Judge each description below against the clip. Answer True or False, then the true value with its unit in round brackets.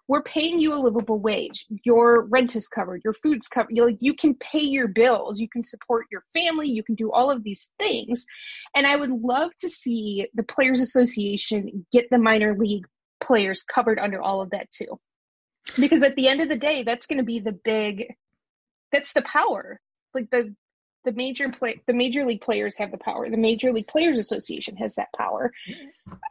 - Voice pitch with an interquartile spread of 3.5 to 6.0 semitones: True (4.1 semitones)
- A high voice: True (245 Hz)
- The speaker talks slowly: False (195 wpm)